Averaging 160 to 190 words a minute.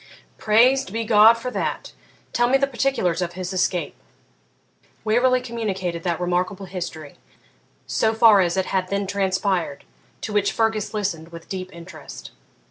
No: average, 145 wpm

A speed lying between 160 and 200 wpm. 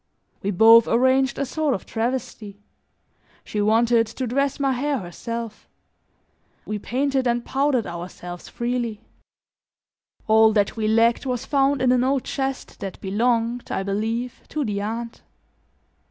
No: average, 140 wpm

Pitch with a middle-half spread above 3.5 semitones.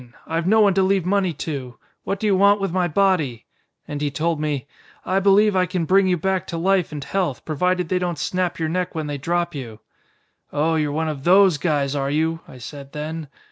Yes: average, 4.1 semitones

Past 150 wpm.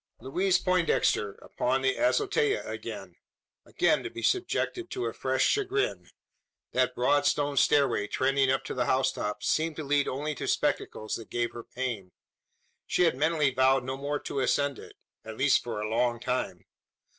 Yes: average, 170 wpm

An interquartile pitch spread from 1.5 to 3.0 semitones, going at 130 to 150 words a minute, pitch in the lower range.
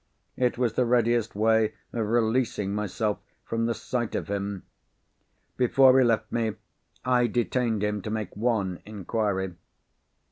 Yes: narrow, 2.4 semitones; average, 140 wpm; low, 110 Hz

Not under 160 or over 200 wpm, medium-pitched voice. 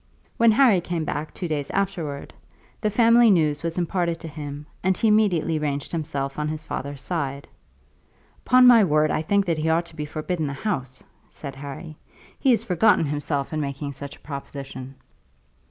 Yes: average, 180 wpm; medium, 155 Hz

